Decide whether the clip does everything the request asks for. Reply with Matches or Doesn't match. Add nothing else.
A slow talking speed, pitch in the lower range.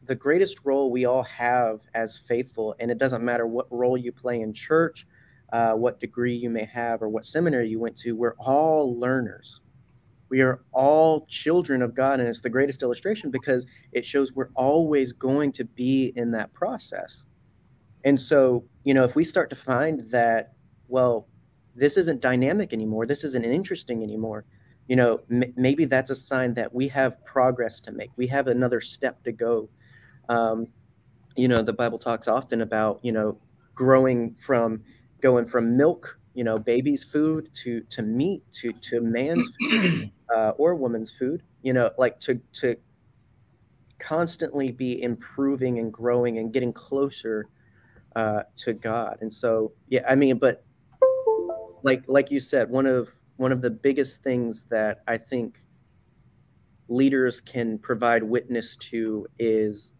Doesn't match